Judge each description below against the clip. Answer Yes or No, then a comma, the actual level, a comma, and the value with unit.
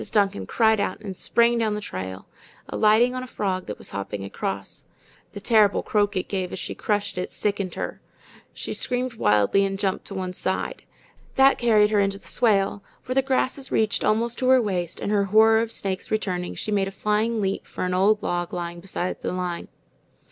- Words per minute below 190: No, average, 200 wpm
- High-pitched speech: Yes, high, 205 Hz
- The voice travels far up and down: No, average, 3.2 semitones